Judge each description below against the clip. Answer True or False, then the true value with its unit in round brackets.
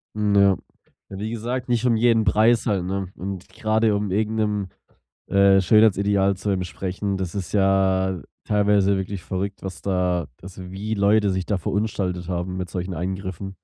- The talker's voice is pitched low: True (100 Hz)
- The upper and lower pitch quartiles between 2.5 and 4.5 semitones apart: False (2.1 semitones)